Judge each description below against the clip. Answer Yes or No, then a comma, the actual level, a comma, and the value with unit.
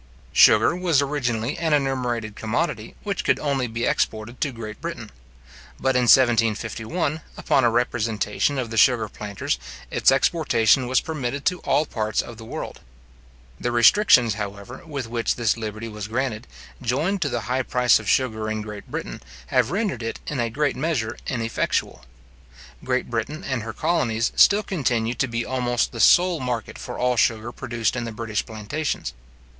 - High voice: No, low, 120 Hz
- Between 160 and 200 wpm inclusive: Yes, average, 165 wpm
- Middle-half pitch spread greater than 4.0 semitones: No, average, 3.7 semitones